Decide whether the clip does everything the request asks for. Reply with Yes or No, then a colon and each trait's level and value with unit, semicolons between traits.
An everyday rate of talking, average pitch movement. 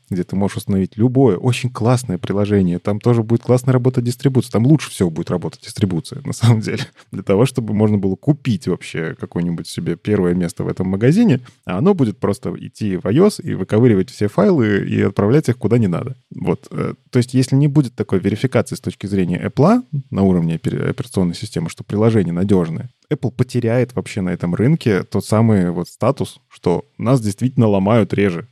No: fast, 185 wpm; average, 4.7 semitones